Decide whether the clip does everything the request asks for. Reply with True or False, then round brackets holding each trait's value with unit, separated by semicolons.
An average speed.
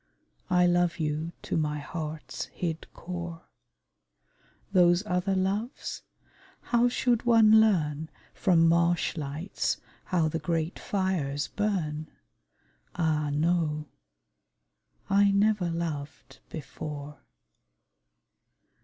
False (90 wpm)